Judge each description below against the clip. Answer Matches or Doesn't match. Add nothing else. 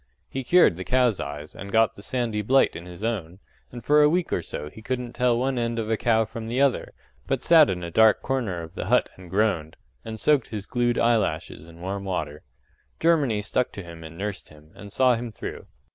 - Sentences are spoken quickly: Matches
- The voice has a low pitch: Matches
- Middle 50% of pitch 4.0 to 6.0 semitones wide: Matches